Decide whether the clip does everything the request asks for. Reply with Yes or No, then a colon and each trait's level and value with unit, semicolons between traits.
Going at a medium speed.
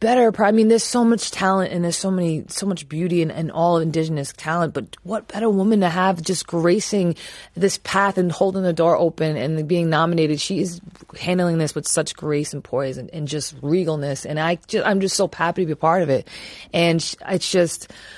No: fast, 215 wpm